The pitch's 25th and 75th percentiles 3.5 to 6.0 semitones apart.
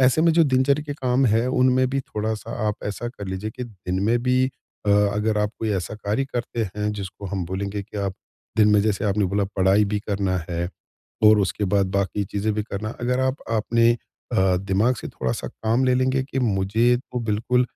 Yes: average, 3.8 semitones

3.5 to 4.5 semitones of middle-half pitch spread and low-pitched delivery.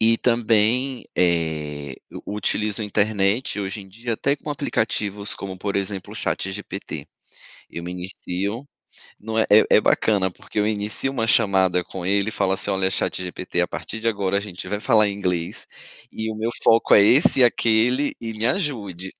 No: average, 3.1 semitones; low, 105 Hz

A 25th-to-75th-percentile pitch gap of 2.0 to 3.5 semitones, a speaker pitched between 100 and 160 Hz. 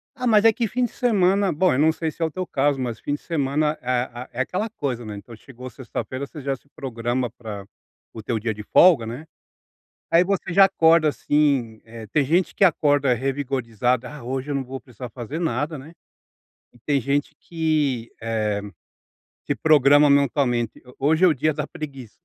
No: average, 4.4 semitones; medium, 140 Hz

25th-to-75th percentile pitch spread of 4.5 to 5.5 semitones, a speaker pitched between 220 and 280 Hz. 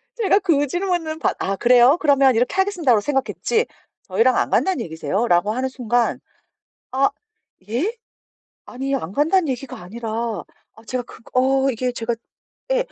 Yes: average, 5.2 semitones; very high, 265 Hz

